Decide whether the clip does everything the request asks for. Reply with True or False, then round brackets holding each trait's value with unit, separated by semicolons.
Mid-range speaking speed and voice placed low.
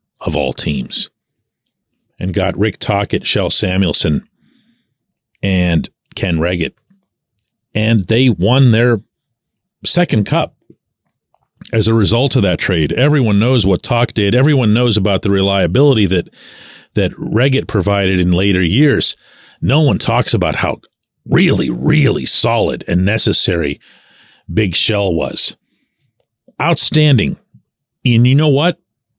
False (120 wpm; 110 Hz)